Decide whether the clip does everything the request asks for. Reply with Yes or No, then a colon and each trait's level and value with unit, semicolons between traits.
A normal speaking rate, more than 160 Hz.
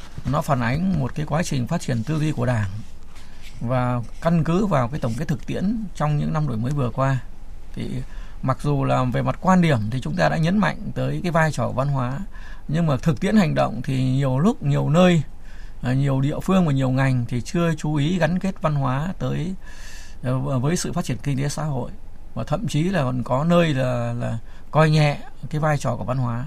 No: average, 230 wpm; medium, 140 Hz